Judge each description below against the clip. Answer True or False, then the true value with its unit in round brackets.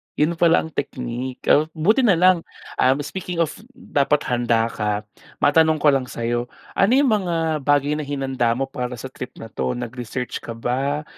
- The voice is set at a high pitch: False (140 Hz)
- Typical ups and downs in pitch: True (4.7 semitones)